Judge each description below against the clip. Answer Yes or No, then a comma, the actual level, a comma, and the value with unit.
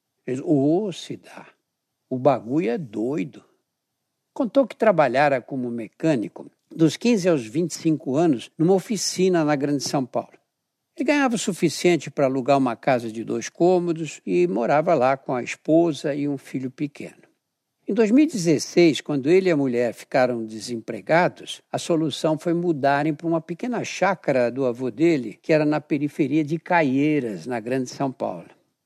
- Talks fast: No, average, 155 wpm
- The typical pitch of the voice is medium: Yes, medium, 155 Hz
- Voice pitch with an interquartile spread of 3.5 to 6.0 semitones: Yes, average, 4.6 semitones